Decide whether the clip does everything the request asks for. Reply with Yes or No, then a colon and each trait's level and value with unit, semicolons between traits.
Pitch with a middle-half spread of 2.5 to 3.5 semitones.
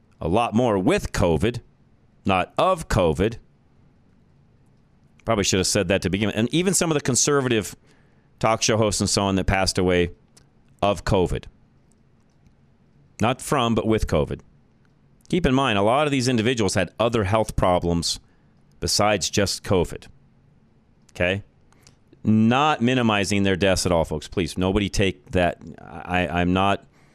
No: average, 4.3 semitones